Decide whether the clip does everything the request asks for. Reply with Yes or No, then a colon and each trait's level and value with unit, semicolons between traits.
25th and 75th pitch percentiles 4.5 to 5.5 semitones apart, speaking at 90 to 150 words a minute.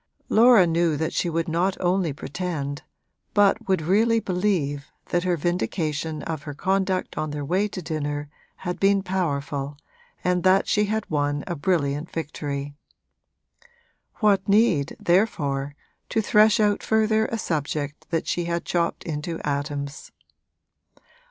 Yes: average, 4.8 semitones; average, 140 wpm